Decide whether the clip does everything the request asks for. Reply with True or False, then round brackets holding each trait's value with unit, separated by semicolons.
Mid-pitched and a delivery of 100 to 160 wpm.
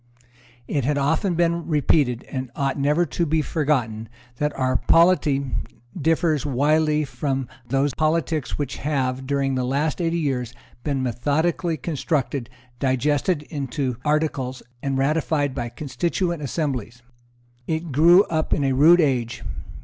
True (145 Hz; 135 wpm)